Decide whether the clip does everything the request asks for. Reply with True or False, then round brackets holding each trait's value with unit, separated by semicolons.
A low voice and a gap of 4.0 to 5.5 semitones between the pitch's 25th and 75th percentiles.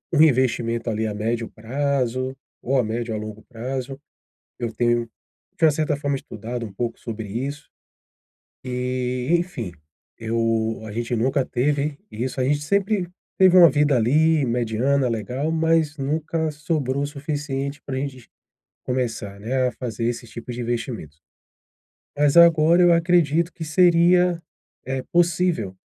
True (130 Hz; 4.6 semitones)